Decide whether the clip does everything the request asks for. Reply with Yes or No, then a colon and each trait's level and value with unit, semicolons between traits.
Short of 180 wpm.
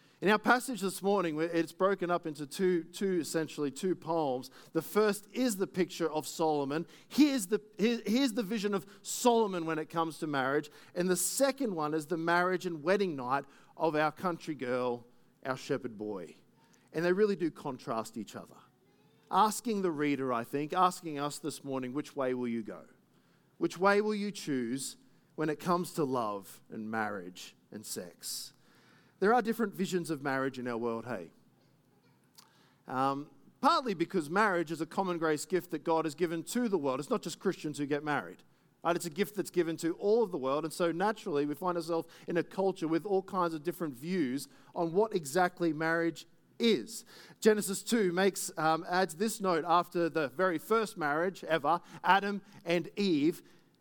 No: average, 185 wpm